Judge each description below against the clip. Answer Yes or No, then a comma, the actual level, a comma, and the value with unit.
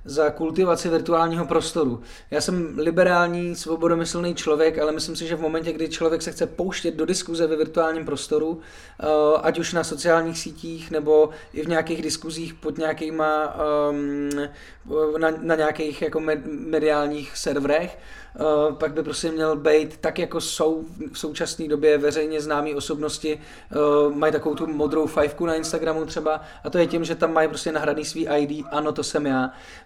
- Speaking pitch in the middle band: Yes, medium, 155 Hz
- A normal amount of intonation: No, narrow, 1.4 semitones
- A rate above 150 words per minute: Yes, fast, 170 wpm